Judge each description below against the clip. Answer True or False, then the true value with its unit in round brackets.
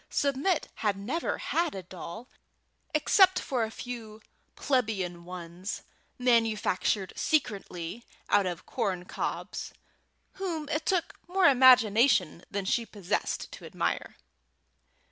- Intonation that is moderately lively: False (6.9 semitones)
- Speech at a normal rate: False (105 wpm)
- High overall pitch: True (225 Hz)